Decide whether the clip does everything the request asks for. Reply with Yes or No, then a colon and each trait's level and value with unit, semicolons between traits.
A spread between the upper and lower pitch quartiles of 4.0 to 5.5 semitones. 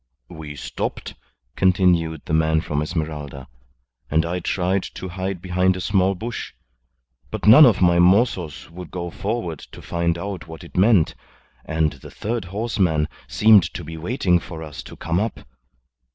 No: average, 3.3 semitones